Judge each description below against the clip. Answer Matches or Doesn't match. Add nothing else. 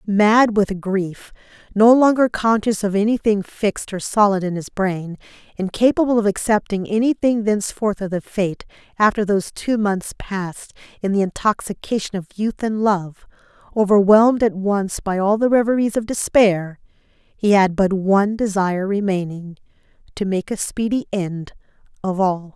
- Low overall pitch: Doesn't match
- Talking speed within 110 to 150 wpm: Matches